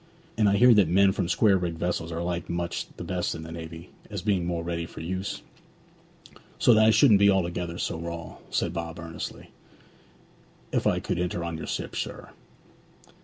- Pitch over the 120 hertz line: No, very low, 85 Hz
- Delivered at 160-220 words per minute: Yes, average, 190 wpm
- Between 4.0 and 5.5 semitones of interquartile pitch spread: No, narrow, 2.6 semitones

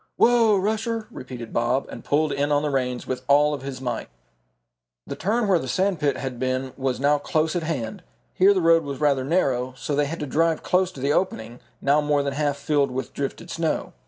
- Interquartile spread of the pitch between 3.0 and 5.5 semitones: Yes, average, 4.0 semitones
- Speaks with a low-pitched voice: No, medium, 145 Hz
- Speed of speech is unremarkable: No, fast, 215 wpm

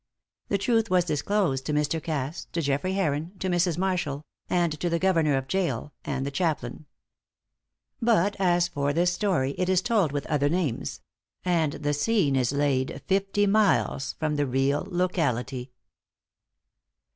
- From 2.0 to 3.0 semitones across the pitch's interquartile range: No, average, 4.7 semitones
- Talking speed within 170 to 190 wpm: No, average, 155 wpm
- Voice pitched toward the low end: No, medium, 160 Hz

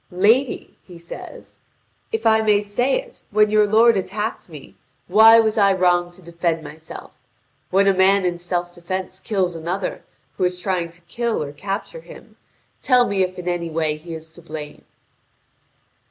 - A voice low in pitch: No, medium, 185 Hz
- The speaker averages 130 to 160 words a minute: No, average, 170 wpm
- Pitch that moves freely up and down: No, average, 3.7 semitones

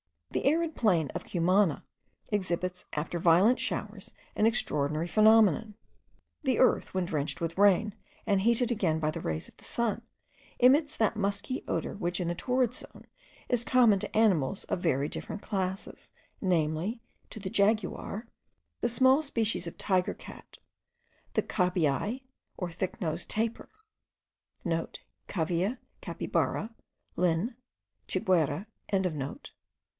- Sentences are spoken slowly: Yes, slow, 130 wpm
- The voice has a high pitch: Yes, high, 195 Hz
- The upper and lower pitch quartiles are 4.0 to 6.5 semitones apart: Yes, average, 4.9 semitones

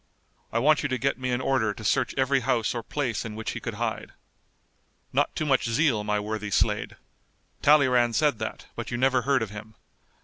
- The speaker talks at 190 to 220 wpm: Yes, fast, 205 wpm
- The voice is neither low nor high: No, low, 120 Hz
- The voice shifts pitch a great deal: No, average, 3.5 semitones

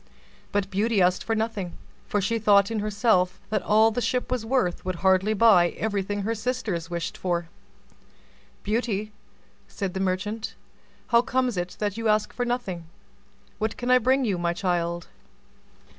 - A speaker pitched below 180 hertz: No, high, 210 Hz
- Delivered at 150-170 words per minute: Yes, average, 160 wpm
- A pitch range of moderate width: Yes, average, 3.7 semitones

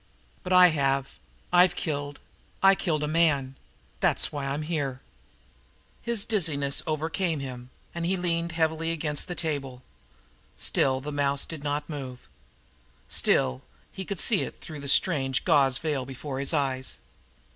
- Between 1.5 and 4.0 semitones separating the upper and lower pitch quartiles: Yes, average, 3.4 semitones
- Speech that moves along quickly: No, average, 155 wpm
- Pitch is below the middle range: No, medium, 150 Hz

